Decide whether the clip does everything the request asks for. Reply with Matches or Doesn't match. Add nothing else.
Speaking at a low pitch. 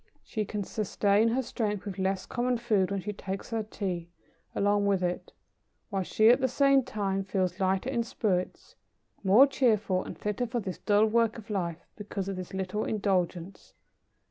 Doesn't match